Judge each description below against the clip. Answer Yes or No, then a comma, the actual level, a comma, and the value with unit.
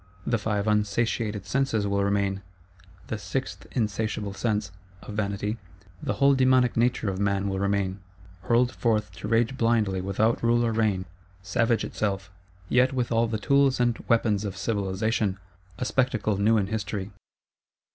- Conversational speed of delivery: Yes, average, 145 wpm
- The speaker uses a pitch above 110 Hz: No, low, 105 Hz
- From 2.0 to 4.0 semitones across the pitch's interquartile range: Yes, average, 2.9 semitones